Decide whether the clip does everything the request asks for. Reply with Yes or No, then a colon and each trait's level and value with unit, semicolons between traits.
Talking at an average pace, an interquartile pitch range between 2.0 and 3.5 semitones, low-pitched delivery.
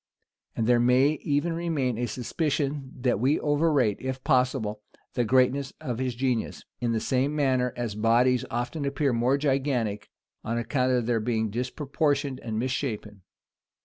Yes: average, 155 wpm; average, 2.9 semitones; low, 130 Hz